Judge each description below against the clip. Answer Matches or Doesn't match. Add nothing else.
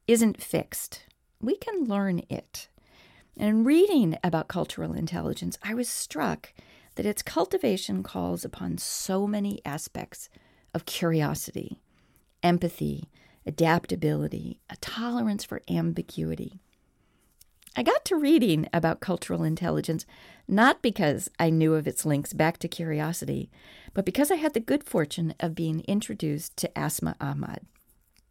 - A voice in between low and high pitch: Matches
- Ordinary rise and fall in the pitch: Doesn't match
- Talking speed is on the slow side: Matches